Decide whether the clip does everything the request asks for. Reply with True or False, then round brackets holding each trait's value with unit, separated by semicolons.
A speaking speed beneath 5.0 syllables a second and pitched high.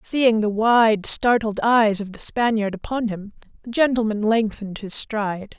True (4.5 syllables/s; 220 Hz)